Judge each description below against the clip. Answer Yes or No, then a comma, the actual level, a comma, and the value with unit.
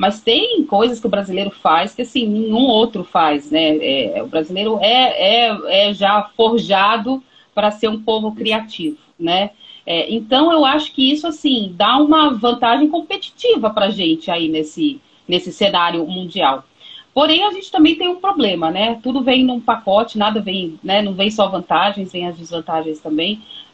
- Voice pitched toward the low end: No, high, 220 Hz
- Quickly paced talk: No, average, 175 wpm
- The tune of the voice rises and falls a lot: Yes, wide, 5.9 semitones